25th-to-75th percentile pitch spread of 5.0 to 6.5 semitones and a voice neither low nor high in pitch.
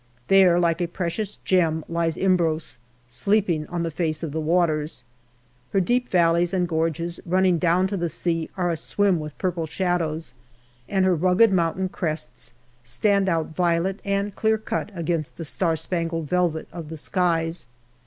No: narrow, 2.5 semitones; medium, 170 Hz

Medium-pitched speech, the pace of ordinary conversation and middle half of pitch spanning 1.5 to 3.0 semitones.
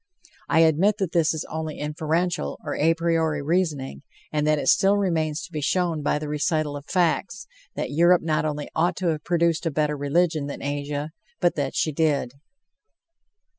Yes: medium, 155 Hz; average, 180 wpm; narrow, 2.5 semitones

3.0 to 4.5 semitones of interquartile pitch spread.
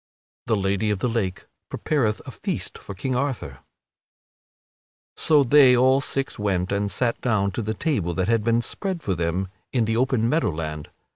No: average, 5.0 semitones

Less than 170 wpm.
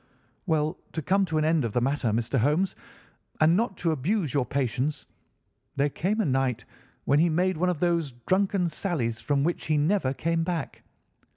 No: average, 185 wpm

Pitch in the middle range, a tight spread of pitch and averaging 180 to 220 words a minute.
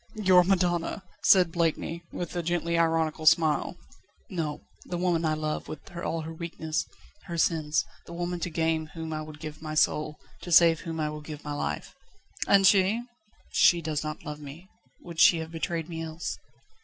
Yes: medium, 165 Hz; narrow, 2.0 semitones; average, 185 wpm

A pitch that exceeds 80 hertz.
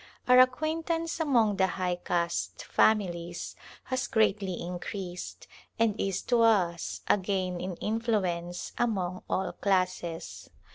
Yes: high, 190 Hz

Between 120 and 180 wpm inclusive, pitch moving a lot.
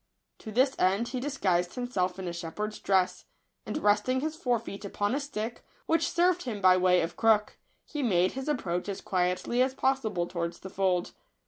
No: average, 195 wpm; wide, 5.9 semitones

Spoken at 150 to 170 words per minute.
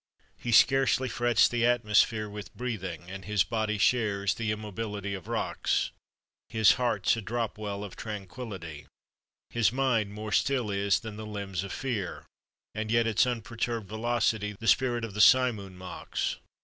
Yes: average, 155 wpm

